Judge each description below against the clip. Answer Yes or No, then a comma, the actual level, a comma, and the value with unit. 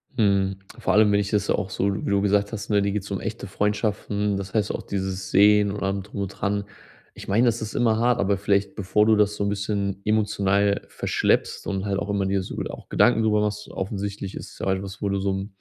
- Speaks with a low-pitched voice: Yes, low, 100 Hz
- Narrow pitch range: Yes, narrow, 1.1 semitones